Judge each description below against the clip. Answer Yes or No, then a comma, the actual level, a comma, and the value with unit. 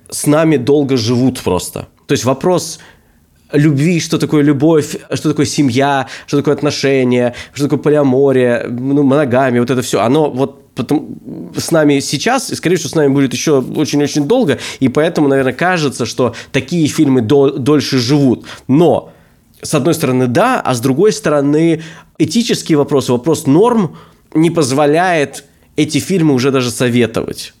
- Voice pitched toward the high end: No, medium, 145 Hz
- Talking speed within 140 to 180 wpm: Yes, average, 155 wpm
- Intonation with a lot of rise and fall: No, average, 2.7 semitones